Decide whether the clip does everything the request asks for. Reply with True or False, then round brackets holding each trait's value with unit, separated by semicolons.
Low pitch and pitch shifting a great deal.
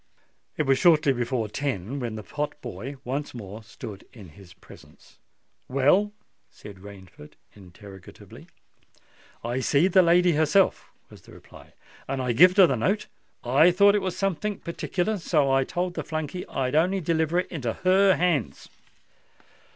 False (145 Hz; 7.1 semitones)